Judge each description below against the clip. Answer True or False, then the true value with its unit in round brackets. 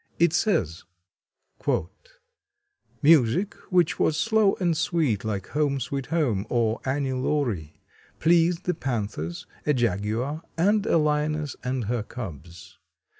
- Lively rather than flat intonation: True (6.8 semitones)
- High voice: False (140 Hz)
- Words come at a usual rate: False (120 wpm)